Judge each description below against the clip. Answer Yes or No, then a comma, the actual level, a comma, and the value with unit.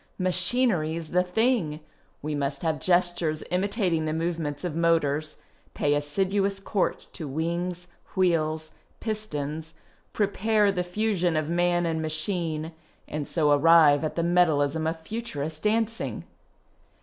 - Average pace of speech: No, slow, 125 wpm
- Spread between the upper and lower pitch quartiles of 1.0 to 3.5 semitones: Yes, average, 3.1 semitones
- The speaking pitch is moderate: Yes, medium, 165 Hz